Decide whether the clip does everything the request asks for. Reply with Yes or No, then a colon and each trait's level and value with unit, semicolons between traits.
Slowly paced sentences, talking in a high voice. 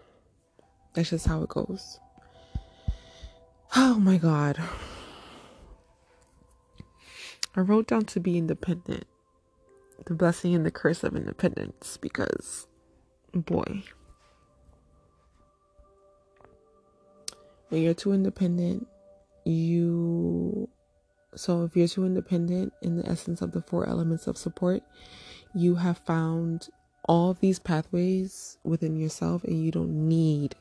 No: slow, 105 wpm; medium, 165 Hz